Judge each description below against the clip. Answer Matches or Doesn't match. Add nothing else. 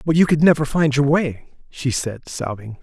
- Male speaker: Matches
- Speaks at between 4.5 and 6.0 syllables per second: Matches